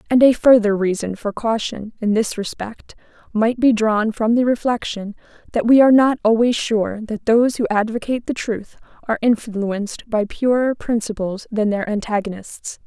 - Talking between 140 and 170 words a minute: Yes, average, 165 wpm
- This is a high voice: Yes, high, 220 Hz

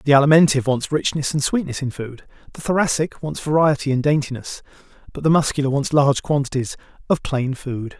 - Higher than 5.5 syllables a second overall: Yes, 5.9 syllables/s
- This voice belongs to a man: Yes, male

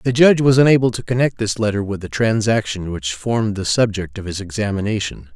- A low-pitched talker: Yes, low, 110 Hz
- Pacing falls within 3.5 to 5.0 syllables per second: No, 6.0 syllables/s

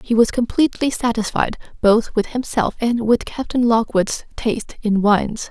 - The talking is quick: No, average, 155 wpm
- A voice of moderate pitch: No, high, 225 Hz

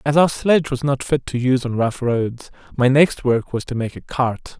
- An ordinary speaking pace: No, fast, 250 wpm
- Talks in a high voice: No, low, 130 Hz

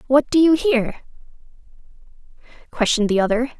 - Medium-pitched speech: No, very high, 255 Hz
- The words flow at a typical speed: No, slow, 115 wpm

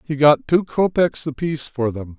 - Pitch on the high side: No, medium, 145 Hz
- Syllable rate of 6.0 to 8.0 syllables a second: No, 4.9 syllables/s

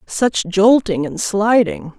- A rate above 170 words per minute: No, slow, 120 wpm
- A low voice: No, high, 210 Hz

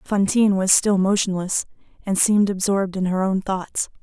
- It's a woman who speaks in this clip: Yes, female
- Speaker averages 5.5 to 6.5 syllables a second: No, 5.2 syllables/s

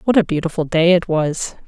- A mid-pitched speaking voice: Yes, medium, 170 Hz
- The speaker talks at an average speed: No, fast, 215 wpm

